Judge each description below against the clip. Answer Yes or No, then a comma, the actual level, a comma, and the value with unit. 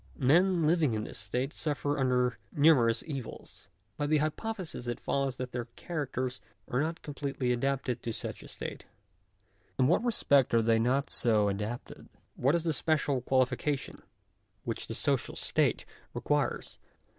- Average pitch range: Yes, average, 3.7 semitones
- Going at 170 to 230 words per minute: No, average, 155 wpm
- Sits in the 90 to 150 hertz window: Yes, low, 135 Hz